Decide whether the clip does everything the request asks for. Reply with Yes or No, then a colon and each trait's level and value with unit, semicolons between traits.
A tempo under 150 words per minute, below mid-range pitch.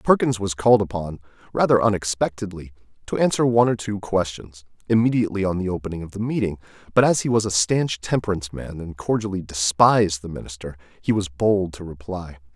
No: average, 175 wpm; very low, 95 Hz